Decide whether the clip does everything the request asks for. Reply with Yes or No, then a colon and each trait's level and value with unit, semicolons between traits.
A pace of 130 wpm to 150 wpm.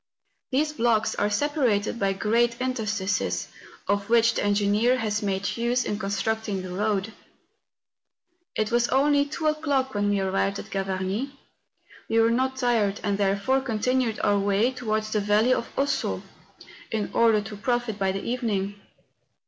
No: average, 160 wpm